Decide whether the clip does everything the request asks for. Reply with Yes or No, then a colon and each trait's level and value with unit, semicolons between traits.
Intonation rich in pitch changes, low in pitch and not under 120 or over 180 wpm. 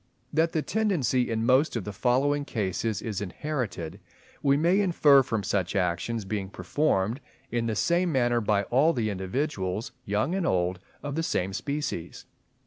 Yes: wide, 6.7 semitones; low, 120 Hz; average, 160 wpm